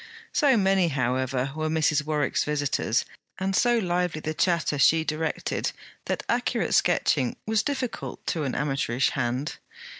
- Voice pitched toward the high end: No, medium, 155 Hz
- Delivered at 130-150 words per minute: Yes, average, 140 wpm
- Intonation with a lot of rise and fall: No, average, 4.8 semitones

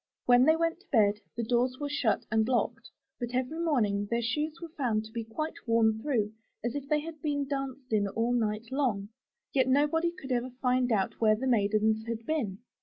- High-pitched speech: Yes, high, 245 Hz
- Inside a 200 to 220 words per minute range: Yes, fast, 205 wpm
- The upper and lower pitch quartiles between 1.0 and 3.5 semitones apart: No, average, 4.5 semitones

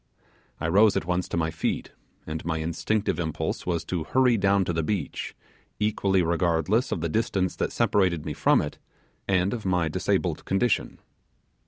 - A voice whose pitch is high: No, very low, 90 Hz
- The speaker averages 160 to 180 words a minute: Yes, average, 170 wpm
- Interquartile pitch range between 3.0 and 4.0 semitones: Yes, average, 3.5 semitones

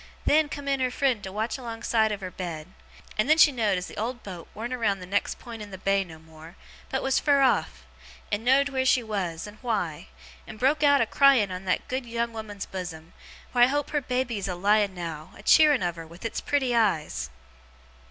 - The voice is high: Yes, high, 220 Hz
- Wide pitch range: Yes, wide, 5.8 semitones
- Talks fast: Yes, fast, 225 wpm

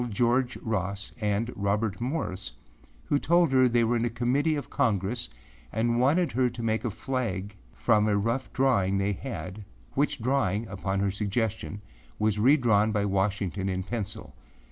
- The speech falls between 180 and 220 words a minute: No, average, 155 wpm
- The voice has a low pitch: Yes, low, 110 Hz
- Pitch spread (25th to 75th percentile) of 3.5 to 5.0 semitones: Yes, average, 3.8 semitones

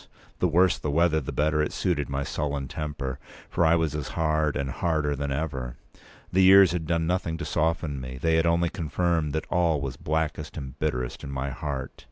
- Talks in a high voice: No, very low, 75 Hz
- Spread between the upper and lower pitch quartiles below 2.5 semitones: No, average, 2.9 semitones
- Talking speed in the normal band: No, fast, 210 wpm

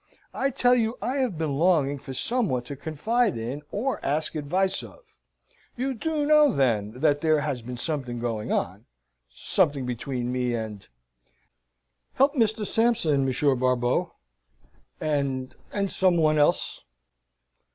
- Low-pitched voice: No, medium, 150 Hz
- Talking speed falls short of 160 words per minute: Yes, average, 140 wpm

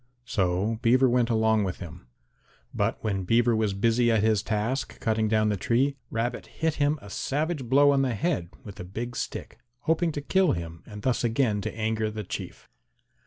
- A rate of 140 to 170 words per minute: No, average, 190 wpm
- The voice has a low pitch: Yes, low, 115 Hz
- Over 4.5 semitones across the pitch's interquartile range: No, average, 3.8 semitones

